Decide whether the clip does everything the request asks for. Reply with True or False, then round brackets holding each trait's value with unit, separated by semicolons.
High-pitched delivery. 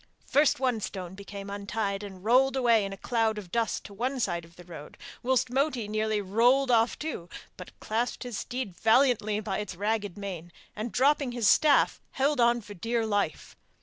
True (220 Hz)